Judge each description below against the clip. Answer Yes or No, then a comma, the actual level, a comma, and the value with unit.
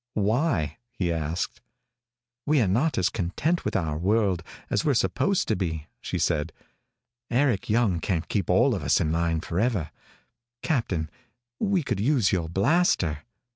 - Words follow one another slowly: No, average, 145 wpm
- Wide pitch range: Yes, wide, 6.6 semitones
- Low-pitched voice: Yes, very low, 95 Hz